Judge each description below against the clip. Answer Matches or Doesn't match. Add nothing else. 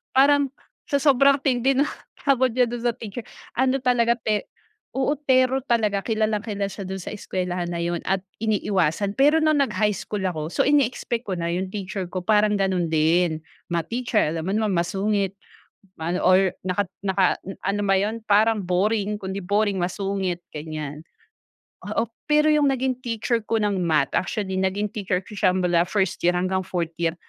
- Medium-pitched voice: Doesn't match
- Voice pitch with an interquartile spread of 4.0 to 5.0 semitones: Matches